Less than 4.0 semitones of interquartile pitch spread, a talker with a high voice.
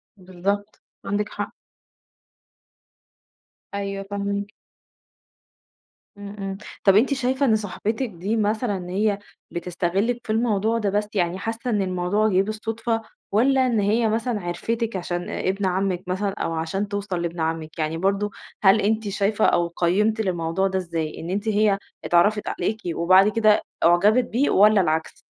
Yes: average, 3.0 semitones; high, 200 Hz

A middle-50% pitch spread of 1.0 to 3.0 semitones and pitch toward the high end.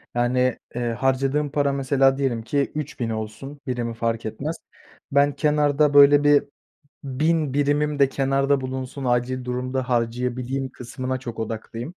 No: narrow, 2.6 semitones; low, 135 Hz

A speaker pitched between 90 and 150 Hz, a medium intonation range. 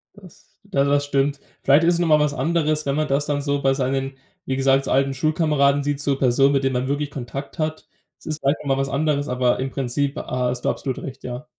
No: medium, 140 Hz; narrow, 1.9 semitones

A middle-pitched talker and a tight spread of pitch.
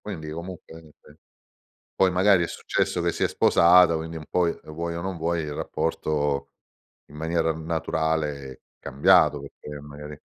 No: very low, 80 Hz; narrow, 2.3 semitones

